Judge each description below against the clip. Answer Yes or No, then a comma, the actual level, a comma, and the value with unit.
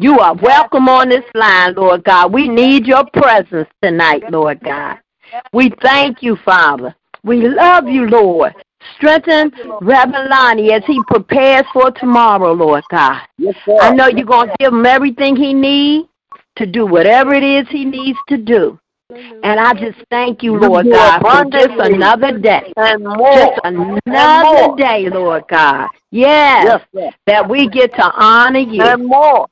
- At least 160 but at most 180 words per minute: No, average, 150 wpm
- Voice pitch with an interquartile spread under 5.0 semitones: Yes, average, 4.1 semitones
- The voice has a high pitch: Yes, very high, 255 Hz